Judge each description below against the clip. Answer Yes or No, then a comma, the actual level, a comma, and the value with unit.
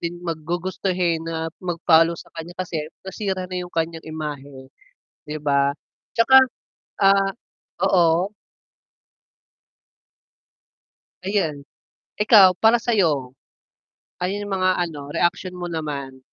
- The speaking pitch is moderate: Yes, medium, 170 Hz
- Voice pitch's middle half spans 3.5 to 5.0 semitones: No, average, 3.0 semitones